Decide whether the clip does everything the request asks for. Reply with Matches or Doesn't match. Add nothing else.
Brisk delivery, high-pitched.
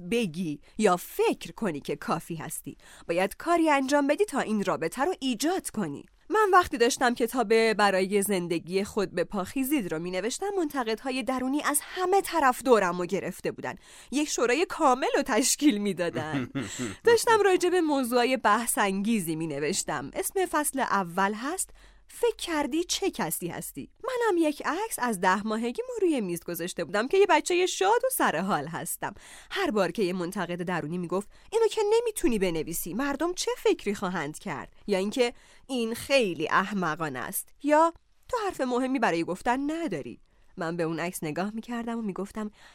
Matches